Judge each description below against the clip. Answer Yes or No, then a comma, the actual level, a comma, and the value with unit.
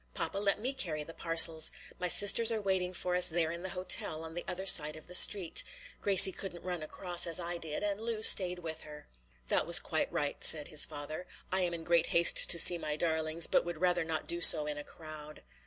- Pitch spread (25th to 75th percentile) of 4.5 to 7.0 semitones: No, narrow, 2.5 semitones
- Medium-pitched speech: Yes, medium, 170 Hz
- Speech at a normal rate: No, fast, 230 wpm